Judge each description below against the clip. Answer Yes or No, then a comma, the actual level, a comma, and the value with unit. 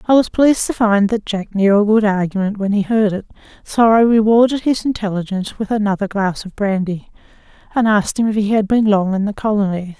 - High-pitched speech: Yes, high, 210 Hz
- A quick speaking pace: Yes, fast, 215 wpm